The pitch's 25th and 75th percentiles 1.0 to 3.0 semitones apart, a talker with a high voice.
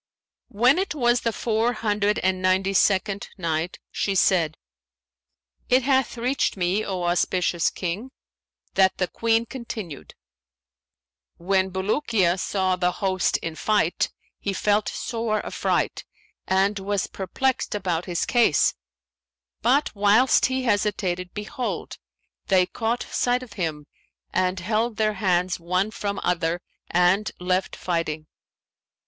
No: average, 3.8 semitones; high, 195 Hz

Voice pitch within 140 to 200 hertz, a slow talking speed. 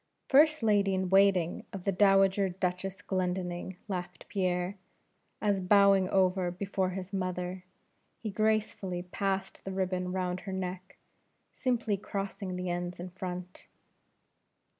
Yes: high, 190 Hz; slow, 125 wpm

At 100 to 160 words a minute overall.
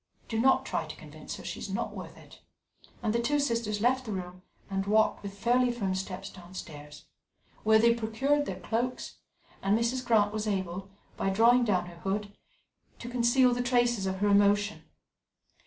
No: average, 180 wpm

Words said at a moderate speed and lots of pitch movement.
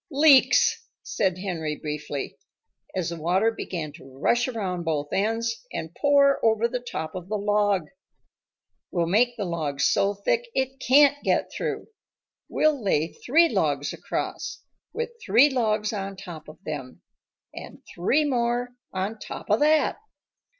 Yes: average, 145 wpm; wide, 6.5 semitones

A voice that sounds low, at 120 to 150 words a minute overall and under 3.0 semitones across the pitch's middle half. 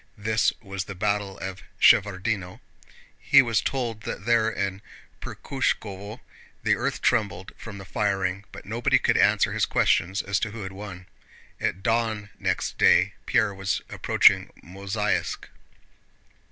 Yes: low, 100 Hz; average, 140 wpm; narrow, 2.5 semitones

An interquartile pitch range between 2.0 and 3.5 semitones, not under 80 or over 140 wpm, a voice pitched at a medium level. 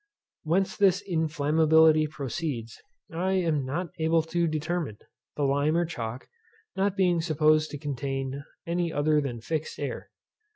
Yes: average, 3.0 semitones; slow, 135 wpm; medium, 155 Hz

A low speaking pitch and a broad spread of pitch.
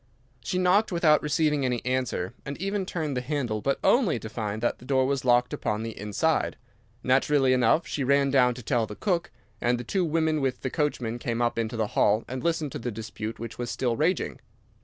No: low, 130 Hz; average, 4.6 semitones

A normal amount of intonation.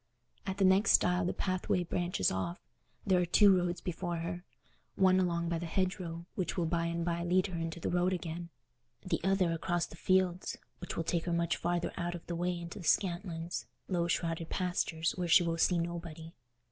No: narrow, 1.4 semitones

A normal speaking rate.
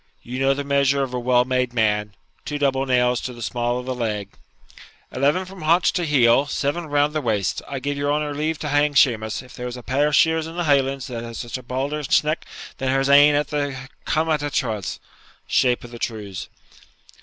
No: fast, 215 wpm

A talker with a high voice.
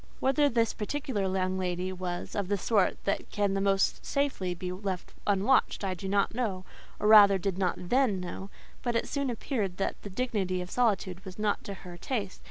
Yes: high, 195 Hz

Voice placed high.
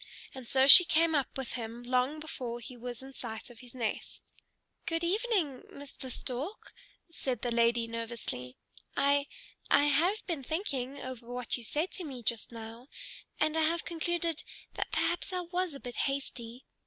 Yes: very high, 265 Hz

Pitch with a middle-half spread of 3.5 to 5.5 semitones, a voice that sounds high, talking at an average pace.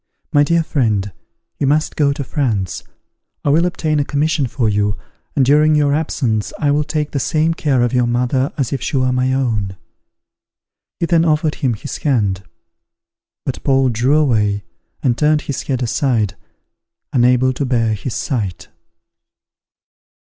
No: average, 4.0 semitones; low, 135 Hz; average, 160 wpm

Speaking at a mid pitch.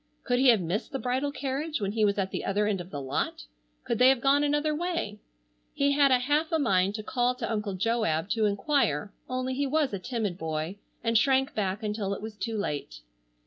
No: high, 225 Hz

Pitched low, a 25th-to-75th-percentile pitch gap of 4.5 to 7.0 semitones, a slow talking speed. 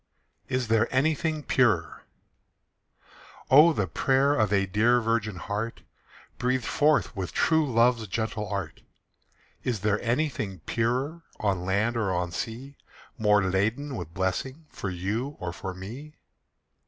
Yes: low, 115 Hz; average, 5.2 semitones; slow, 130 wpm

